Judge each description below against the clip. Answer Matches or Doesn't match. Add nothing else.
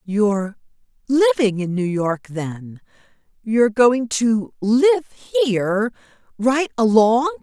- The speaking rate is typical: Doesn't match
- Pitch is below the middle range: Doesn't match